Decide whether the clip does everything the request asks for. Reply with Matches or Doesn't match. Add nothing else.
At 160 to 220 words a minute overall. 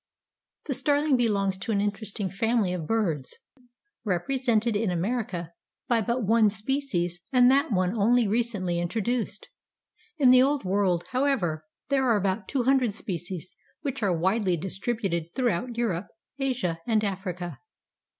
Doesn't match